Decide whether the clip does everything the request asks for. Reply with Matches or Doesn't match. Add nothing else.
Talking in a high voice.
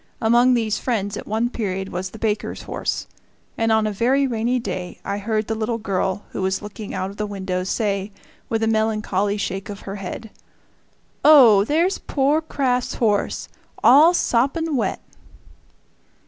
Matches